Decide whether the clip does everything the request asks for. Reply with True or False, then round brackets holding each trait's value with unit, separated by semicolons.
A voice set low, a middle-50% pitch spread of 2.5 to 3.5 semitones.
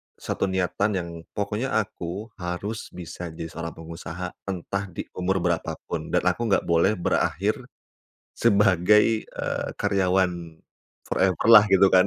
True (95 Hz; 2.8 semitones)